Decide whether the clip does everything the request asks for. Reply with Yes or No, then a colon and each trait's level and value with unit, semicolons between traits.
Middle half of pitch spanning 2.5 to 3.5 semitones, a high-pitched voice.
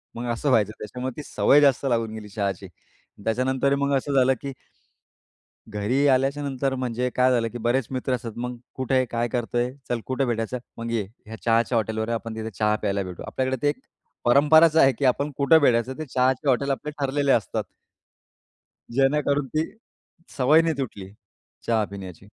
No: average, 3.2 semitones; low, 125 Hz